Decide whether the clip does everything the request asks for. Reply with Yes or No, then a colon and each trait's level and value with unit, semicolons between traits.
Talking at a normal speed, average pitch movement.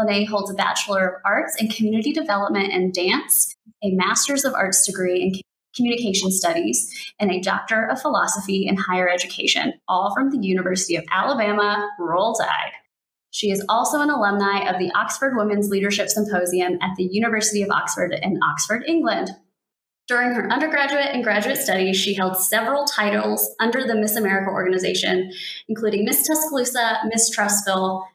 Yes: average, 160 wpm; average, 3.8 semitones